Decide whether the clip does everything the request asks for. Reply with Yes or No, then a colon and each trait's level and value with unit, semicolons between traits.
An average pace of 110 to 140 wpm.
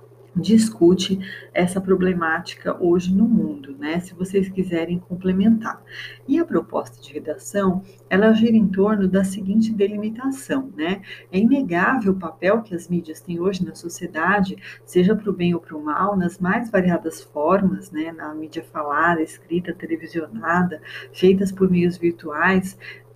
No: average, 150 wpm